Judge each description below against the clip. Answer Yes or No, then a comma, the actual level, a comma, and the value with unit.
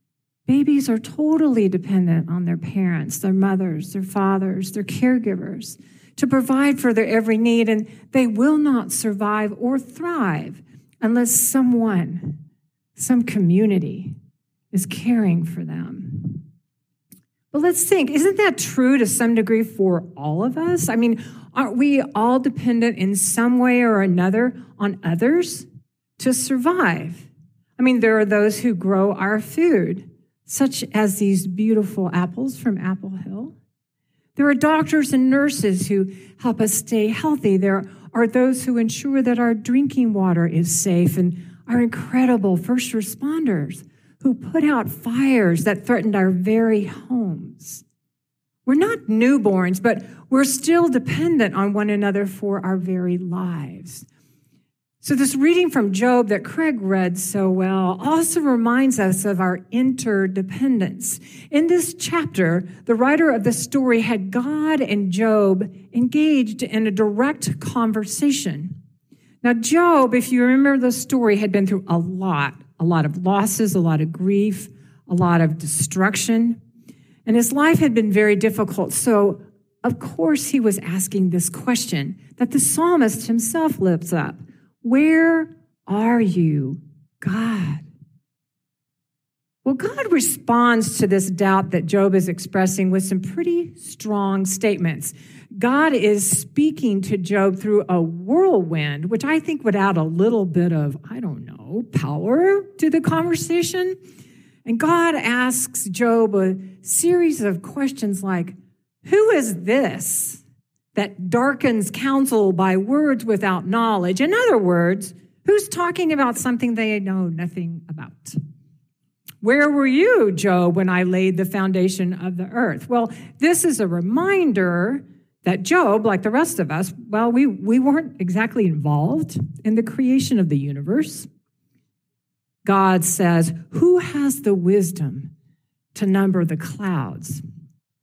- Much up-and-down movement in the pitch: Yes, wide, 5.7 semitones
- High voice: Yes, high, 210 Hz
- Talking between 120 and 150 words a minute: Yes, average, 140 wpm